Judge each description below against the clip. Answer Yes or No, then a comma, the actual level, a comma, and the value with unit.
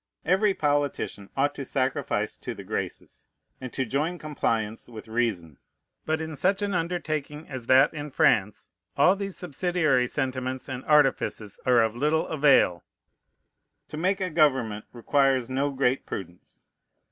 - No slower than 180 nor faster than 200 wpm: No, average, 145 wpm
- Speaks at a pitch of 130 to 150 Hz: Yes, medium, 140 Hz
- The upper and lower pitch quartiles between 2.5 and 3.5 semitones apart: No, average, 4.3 semitones